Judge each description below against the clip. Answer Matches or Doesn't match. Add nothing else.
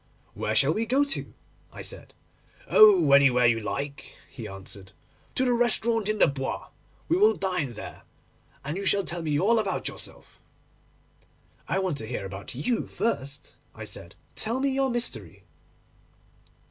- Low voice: Doesn't match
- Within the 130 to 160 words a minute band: Matches